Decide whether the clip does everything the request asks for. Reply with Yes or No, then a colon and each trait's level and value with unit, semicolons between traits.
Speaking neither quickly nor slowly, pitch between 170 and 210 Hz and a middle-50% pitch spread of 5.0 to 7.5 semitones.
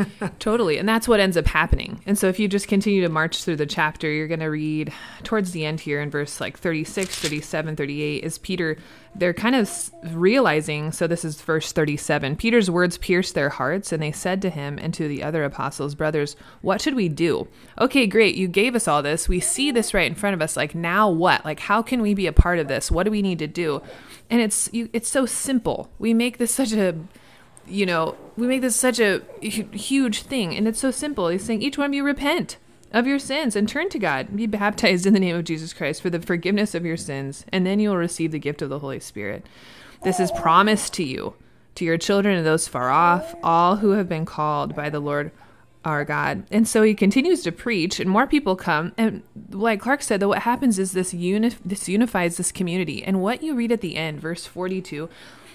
No: fast, 230 wpm; medium, 185 Hz; wide, 5.4 semitones